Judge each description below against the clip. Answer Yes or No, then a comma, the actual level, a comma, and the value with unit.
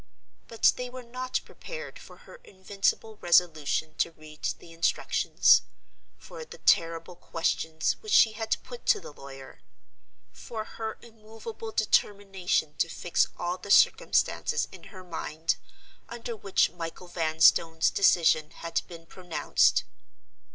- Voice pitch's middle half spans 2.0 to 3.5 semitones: No, average, 5.2 semitones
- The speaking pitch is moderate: Yes, medium, 180 Hz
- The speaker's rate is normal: No, slow, 130 wpm